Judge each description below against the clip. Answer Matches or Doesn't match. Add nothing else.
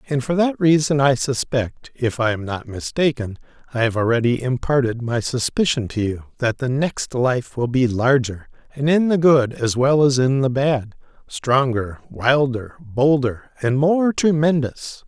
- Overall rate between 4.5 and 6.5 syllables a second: Doesn't match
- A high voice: Doesn't match